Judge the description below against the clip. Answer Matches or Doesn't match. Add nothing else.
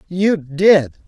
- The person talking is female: Doesn't match